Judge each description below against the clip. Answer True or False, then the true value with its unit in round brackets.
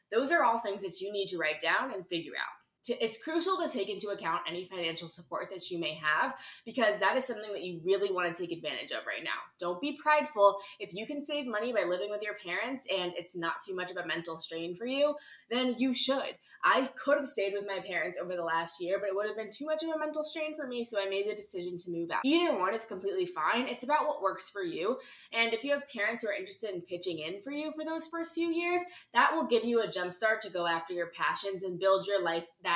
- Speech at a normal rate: False (265 wpm)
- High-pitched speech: True (200 Hz)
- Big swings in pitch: True (7.6 semitones)